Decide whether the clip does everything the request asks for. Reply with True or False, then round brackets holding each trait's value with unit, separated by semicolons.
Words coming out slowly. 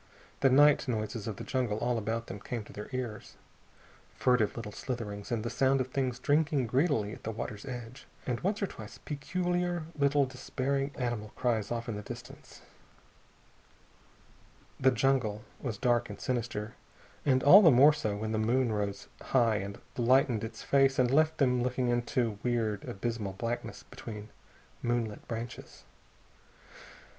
False (160 wpm)